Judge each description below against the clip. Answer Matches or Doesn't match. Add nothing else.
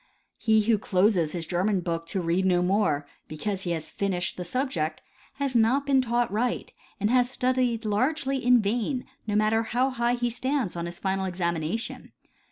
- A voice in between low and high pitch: Doesn't match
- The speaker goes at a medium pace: Matches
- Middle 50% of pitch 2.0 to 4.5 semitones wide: Doesn't match